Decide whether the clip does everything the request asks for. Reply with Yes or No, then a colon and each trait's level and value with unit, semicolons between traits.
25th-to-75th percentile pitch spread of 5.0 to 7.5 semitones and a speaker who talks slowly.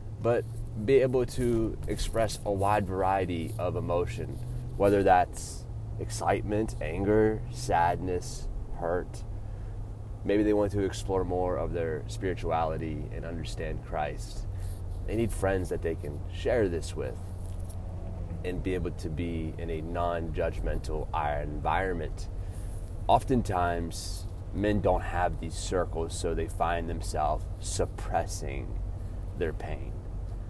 No: average, 3.2 semitones; slow, 120 wpm